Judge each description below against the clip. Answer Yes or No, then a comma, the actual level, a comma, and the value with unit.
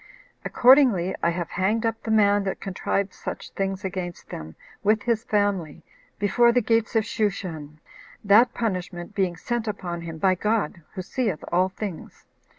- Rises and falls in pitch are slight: No, average, 3.8 semitones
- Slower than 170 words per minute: Yes, average, 155 wpm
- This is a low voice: No, high, 200 Hz